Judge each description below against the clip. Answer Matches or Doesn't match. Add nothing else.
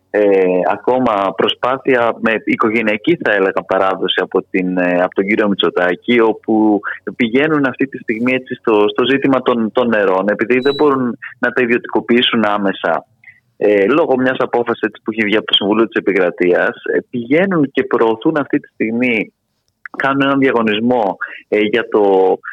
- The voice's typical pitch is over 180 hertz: Doesn't match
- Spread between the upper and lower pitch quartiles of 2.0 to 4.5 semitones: Matches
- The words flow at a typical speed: Matches